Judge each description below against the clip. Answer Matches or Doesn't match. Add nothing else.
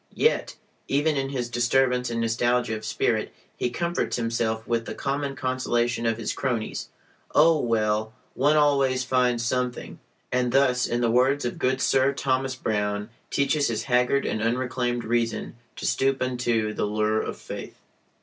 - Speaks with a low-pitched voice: Matches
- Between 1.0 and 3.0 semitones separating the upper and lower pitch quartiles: Matches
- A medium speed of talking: Matches